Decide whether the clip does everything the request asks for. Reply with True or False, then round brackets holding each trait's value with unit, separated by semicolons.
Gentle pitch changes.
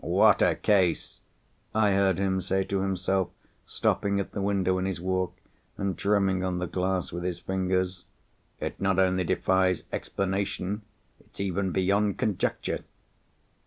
True (1.1 semitones)